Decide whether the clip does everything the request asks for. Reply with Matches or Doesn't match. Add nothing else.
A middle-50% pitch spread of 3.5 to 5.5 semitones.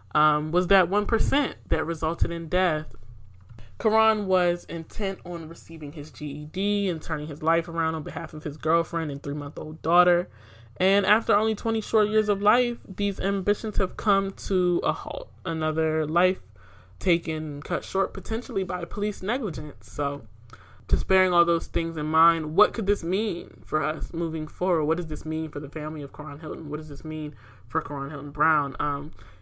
Matches